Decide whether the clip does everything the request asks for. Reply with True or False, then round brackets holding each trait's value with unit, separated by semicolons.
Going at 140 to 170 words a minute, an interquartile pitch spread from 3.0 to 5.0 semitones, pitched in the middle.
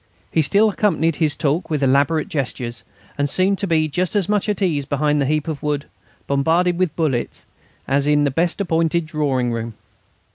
False (185 wpm; 3.5 semitones; 155 Hz)